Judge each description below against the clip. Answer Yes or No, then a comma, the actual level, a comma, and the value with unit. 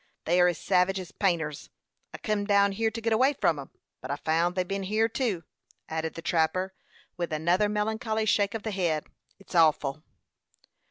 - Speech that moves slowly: No, average, 185 wpm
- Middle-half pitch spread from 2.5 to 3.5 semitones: No, average, 4.3 semitones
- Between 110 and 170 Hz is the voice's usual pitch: No, medium, 185 Hz